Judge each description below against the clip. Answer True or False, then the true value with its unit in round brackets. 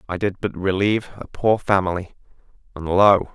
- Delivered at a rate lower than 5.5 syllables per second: True (5.1 syllables/s)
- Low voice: True (95 Hz)